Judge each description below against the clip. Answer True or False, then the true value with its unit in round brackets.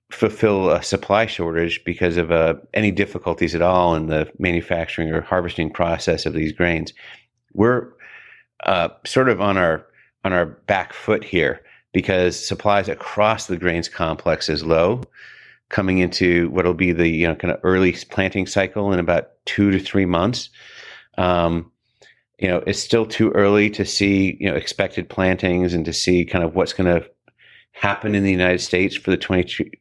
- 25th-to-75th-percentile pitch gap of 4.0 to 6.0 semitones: False (2.5 semitones)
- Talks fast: False (175 wpm)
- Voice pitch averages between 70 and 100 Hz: True (90 Hz)